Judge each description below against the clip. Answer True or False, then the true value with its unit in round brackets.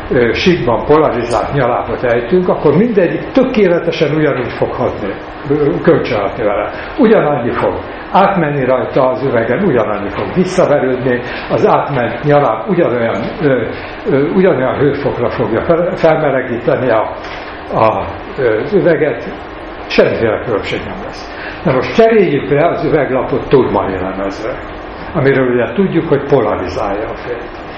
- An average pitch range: False (6.1 semitones)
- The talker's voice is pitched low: False (145 Hz)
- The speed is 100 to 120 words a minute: True (110 wpm)